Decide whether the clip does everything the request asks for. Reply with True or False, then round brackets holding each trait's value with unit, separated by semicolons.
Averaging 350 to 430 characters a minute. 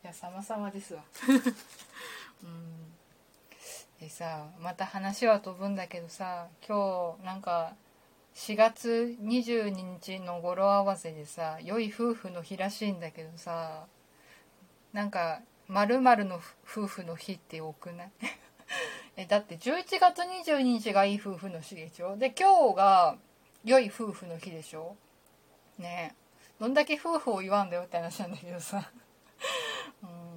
False (235 characters per minute)